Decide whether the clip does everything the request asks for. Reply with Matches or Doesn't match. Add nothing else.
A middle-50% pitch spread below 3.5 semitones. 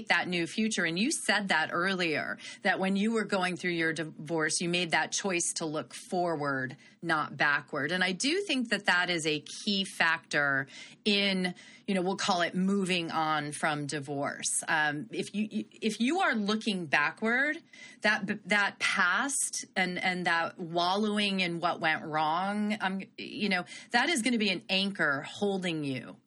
Doesn't match